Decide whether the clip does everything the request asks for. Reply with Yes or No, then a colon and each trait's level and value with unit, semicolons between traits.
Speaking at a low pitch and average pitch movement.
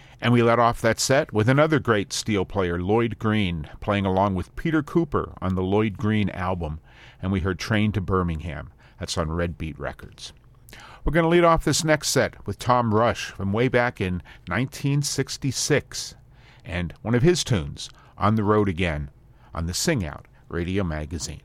No: low, 105 Hz; wide, 6.0 semitones